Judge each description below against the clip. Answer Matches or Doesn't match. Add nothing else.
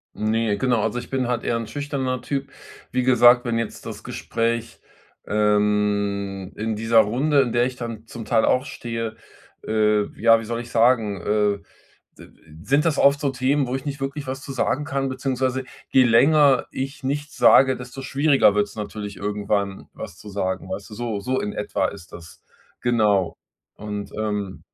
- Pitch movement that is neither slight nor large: Matches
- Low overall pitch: Matches